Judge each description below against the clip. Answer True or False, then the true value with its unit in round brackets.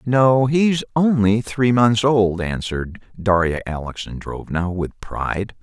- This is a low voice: True (110 Hz)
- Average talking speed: False (115 wpm)